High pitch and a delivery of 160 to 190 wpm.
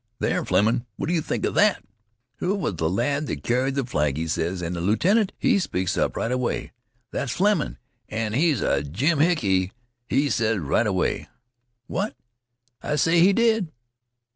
No: low, 120 Hz; average, 170 wpm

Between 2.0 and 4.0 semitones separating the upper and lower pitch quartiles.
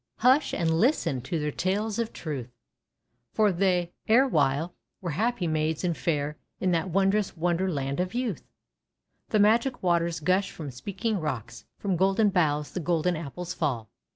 No: average, 4.5 semitones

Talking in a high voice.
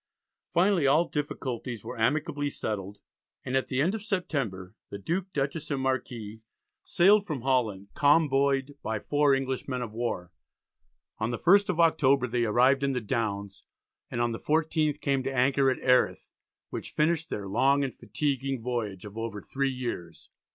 No: low, 135 Hz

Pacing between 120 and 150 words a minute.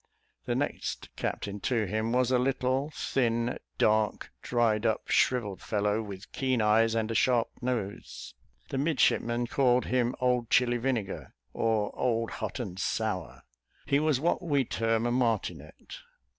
Yes: average, 145 wpm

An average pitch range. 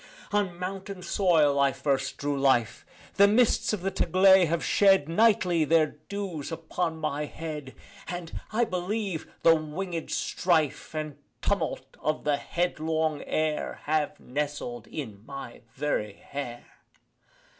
Yes: average, 4.1 semitones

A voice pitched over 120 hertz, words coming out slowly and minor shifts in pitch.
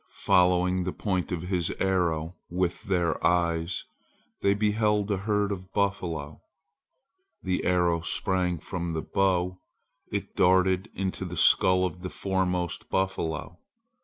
No: very low, 90 Hz; slow, 130 wpm; narrow, 1.5 semitones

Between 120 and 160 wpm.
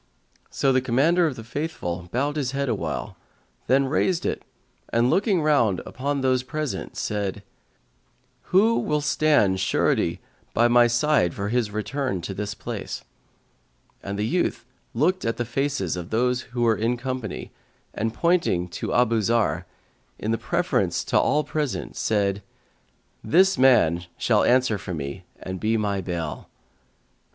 Yes: average, 145 wpm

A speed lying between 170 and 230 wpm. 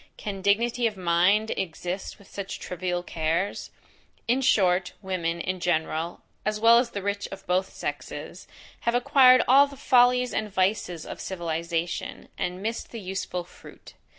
No: average, 150 wpm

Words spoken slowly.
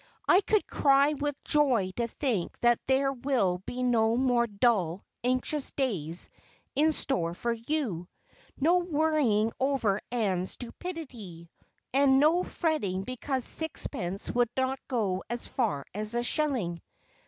Yes: slow, 130 wpm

